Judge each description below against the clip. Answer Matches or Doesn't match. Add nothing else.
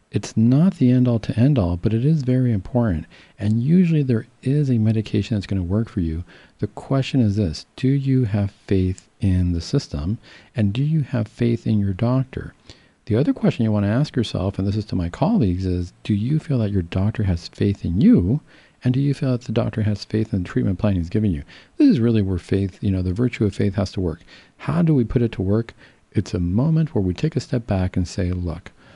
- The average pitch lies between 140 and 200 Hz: Doesn't match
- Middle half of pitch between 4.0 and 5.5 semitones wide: Matches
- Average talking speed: Doesn't match